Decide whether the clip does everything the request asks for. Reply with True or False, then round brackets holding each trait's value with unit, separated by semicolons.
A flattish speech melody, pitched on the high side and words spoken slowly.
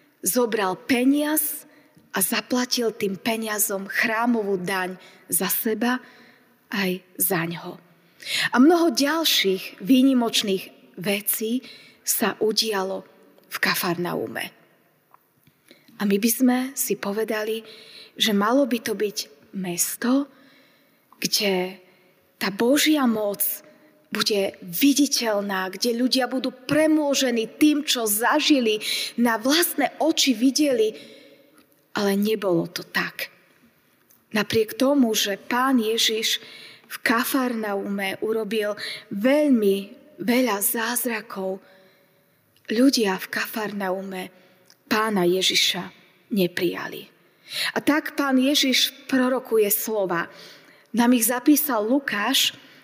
False (4.9 semitones; 225 Hz; 95 wpm)